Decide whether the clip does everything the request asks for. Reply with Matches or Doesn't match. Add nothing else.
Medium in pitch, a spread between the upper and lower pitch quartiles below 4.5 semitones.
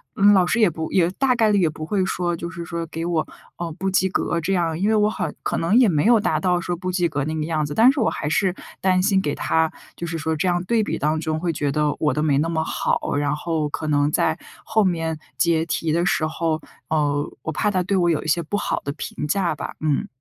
Matches